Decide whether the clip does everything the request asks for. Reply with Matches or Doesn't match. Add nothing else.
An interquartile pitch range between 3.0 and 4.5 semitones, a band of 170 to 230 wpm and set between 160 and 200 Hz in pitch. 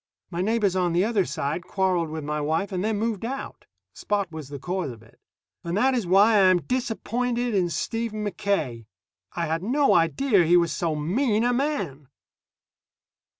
Doesn't match